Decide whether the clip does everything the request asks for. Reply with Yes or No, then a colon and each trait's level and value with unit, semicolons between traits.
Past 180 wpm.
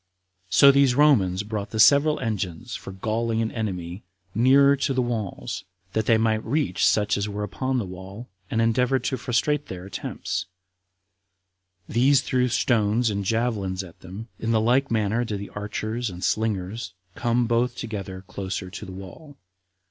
No: average, 165 wpm